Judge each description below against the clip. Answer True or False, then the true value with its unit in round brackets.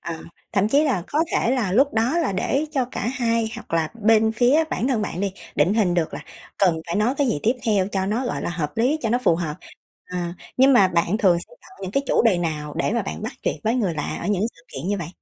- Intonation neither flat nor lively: False (5.8 semitones)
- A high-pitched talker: True (210 Hz)